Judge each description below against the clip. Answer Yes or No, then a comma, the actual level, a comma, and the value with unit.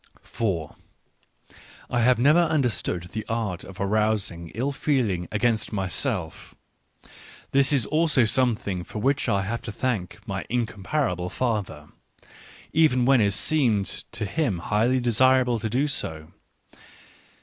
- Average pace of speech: No, slow, 130 wpm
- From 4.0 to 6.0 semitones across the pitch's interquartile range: Yes, average, 4.6 semitones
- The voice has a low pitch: Yes, low, 115 Hz